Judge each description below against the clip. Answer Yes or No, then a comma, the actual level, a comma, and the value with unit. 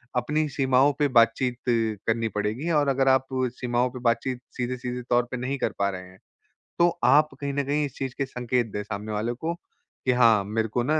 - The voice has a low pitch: Yes, low, 125 Hz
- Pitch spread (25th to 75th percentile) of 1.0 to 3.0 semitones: No, average, 3.4 semitones